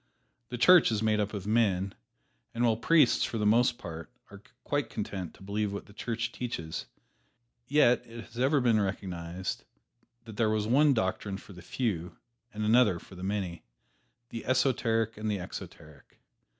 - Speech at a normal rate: Yes, average, 170 wpm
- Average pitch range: Yes, average, 3.6 semitones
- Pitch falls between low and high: No, low, 110 Hz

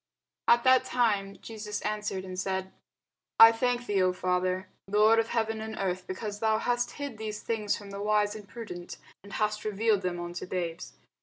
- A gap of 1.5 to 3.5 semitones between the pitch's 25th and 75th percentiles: Yes, average, 2.9 semitones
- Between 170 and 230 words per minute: Yes, average, 180 wpm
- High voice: Yes, high, 210 Hz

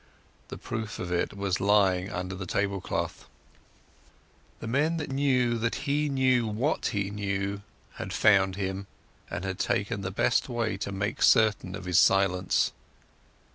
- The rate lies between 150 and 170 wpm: Yes, average, 155 wpm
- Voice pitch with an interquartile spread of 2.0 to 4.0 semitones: Yes, average, 3.6 semitones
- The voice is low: Yes, low, 100 Hz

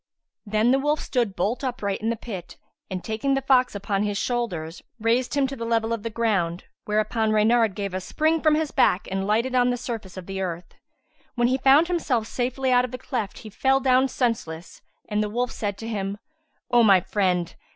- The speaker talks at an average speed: No, fast, 210 wpm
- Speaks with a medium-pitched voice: No, high, 225 Hz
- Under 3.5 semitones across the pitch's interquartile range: No, average, 4.1 semitones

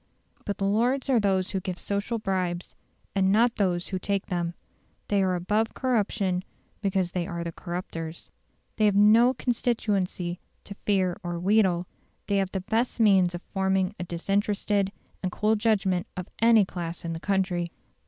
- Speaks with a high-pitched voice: Yes, high, 195 Hz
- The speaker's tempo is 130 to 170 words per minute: Yes, average, 165 wpm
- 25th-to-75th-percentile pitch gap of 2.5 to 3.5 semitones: Yes, average, 2.8 semitones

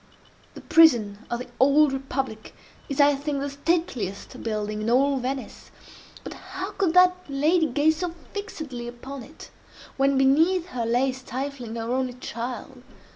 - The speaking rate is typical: Yes, average, 145 wpm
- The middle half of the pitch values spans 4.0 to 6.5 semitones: Yes, average, 4.3 semitones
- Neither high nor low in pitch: No, very high, 270 Hz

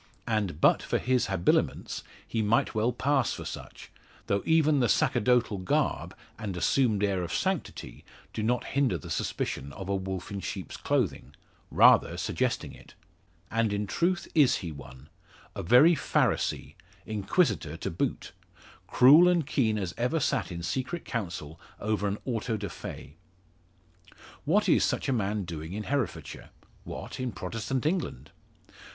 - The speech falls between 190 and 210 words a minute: No, average, 150 wpm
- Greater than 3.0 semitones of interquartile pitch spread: Yes, wide, 5.6 semitones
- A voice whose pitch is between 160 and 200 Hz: No, low, 110 Hz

